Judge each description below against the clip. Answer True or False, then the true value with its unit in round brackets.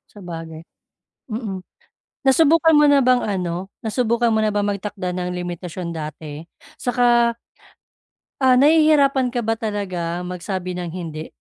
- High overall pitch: True (205 Hz)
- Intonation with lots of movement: True (5.7 semitones)